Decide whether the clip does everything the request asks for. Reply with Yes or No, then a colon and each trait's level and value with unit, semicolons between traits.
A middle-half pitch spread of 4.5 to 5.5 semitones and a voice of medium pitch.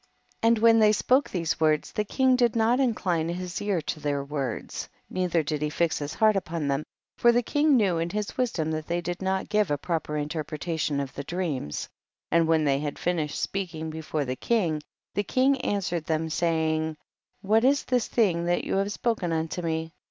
Yes: average, 5.2 semitones; medium, 170 Hz